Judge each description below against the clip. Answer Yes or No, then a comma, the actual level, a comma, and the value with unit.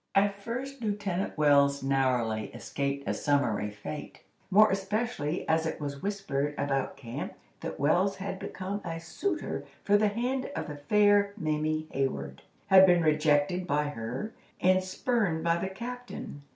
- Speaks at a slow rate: No, average, 150 wpm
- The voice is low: No, medium, 165 Hz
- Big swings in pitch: Yes, wide, 6.1 semitones